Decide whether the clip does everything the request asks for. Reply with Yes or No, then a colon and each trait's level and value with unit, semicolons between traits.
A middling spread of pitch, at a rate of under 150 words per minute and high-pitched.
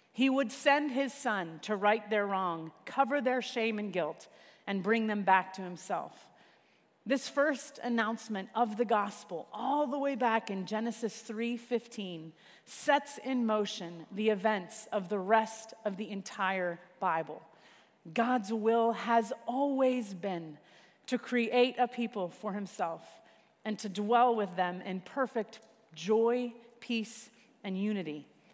Yes: average, 3.5 semitones; average, 140 wpm; high, 220 Hz